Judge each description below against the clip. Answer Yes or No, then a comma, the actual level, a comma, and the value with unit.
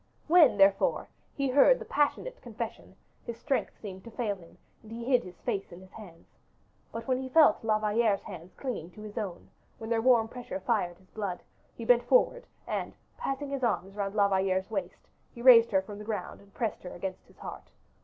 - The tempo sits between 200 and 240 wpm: Yes, fast, 205 wpm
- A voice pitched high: Yes, high, 220 Hz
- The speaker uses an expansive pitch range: No, average, 4.1 semitones